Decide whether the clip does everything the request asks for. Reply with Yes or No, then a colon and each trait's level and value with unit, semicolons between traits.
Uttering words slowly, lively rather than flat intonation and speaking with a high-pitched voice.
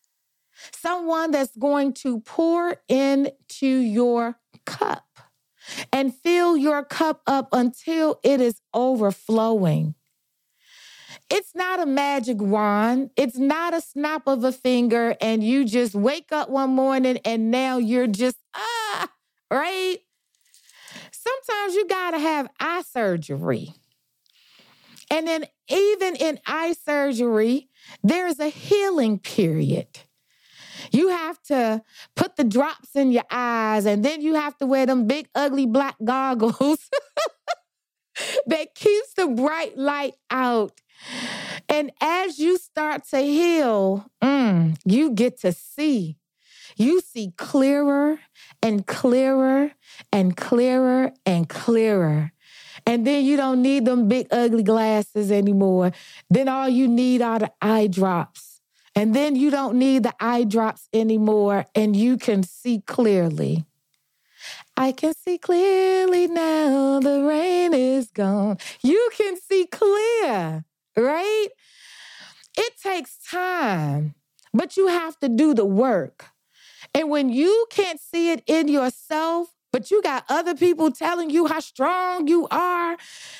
Yes: slow, 130 wpm; wide, 6.0 semitones; very high, 270 Hz